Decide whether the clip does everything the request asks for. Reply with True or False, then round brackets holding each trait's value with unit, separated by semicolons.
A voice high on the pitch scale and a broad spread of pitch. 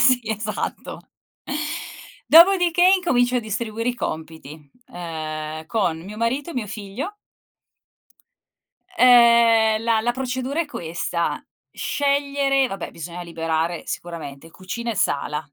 True (220 Hz; 7.3 semitones)